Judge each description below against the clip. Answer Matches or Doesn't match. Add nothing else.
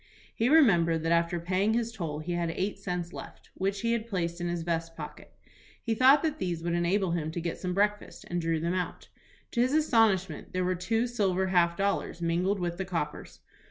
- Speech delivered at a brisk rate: Matches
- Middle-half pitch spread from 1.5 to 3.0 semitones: Doesn't match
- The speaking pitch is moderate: Matches